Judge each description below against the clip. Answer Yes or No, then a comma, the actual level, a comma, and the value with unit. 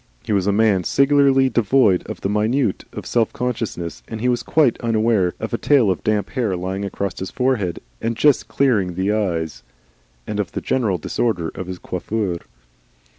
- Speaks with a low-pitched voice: Yes, low, 110 Hz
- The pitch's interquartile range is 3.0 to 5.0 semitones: Yes, average, 4.5 semitones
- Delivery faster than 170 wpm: Yes, average, 180 wpm